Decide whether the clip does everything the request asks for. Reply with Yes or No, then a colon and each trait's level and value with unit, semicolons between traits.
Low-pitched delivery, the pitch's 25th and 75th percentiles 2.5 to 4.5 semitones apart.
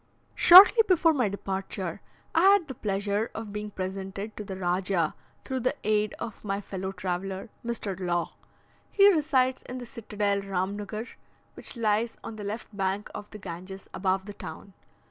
No: high, 205 Hz; average, 3.3 semitones